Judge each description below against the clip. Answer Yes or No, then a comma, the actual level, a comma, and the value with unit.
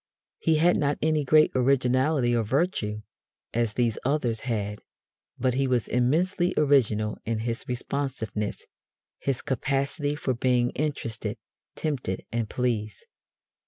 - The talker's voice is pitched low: Yes, low, 125 Hz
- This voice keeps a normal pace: No, slow, 125 wpm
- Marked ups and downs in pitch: No, average, 3.9 semitones